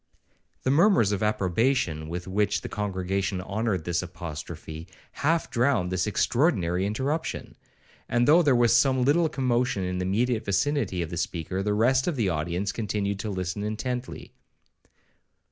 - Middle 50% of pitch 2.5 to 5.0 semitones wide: No, wide, 5.6 semitones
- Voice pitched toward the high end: No, low, 105 Hz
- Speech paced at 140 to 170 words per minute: Yes, average, 150 wpm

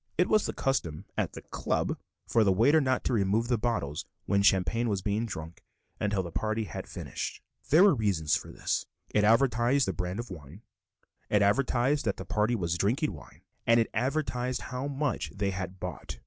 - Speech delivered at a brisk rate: No, average, 190 wpm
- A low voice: Yes, low, 110 Hz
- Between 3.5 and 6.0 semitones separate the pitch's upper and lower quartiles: Yes, average, 4.9 semitones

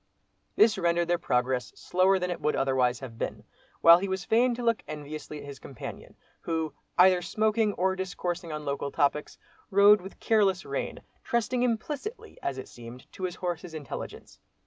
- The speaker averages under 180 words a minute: Yes, average, 170 wpm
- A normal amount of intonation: No, wide, 5.7 semitones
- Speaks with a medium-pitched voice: Yes, medium, 175 Hz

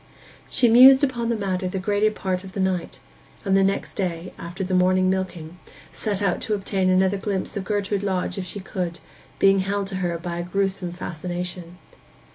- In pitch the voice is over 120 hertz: Yes, high, 190 Hz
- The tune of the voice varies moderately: No, narrow, 1.7 semitones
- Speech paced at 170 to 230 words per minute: Yes, average, 190 wpm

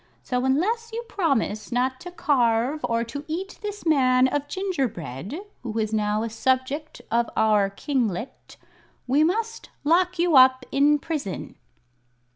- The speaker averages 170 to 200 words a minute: No, average, 140 wpm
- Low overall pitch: No, very high, 265 Hz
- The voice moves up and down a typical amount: No, wide, 6.3 semitones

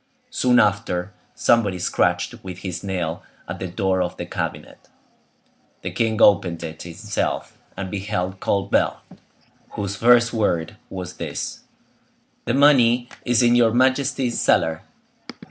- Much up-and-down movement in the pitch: No, average, 4.7 semitones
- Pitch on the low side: Yes, low, 100 Hz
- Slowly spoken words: Yes, slow, 125 wpm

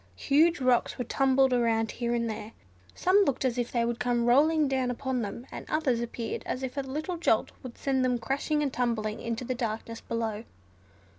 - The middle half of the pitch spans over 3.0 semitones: No, narrow, 2.6 semitones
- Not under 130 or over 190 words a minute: No, average, 200 wpm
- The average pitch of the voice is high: Yes, very high, 250 Hz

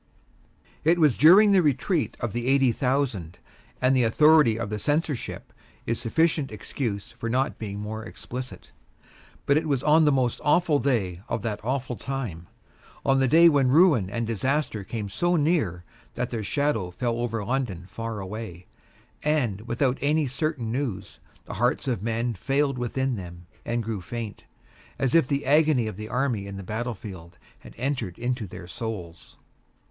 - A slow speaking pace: No, average, 165 wpm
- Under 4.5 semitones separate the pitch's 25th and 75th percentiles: No, average, 4.8 semitones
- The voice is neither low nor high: No, low, 120 Hz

